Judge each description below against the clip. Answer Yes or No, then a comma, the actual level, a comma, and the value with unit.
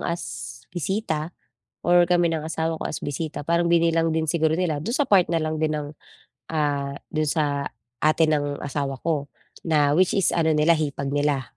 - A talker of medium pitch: Yes, medium, 155 Hz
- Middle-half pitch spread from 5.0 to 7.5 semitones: No, narrow, 2.5 semitones